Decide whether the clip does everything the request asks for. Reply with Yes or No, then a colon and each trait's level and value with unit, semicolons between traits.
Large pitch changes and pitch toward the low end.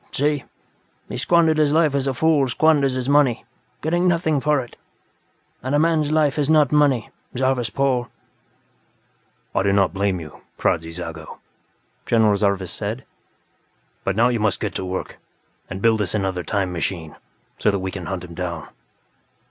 Yes: wide, 7.4 semitones; low, 120 Hz